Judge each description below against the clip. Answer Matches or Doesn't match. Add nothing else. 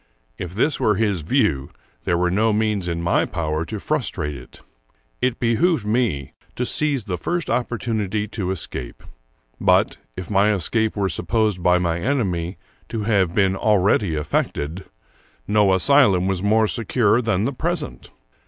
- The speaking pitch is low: Matches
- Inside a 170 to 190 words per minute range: Doesn't match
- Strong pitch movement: Doesn't match